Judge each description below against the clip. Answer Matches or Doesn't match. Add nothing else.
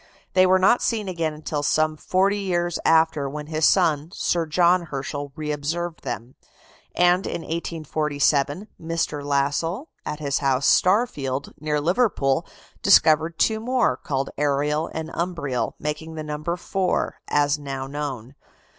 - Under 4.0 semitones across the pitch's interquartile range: Matches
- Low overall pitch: Doesn't match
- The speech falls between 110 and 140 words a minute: Matches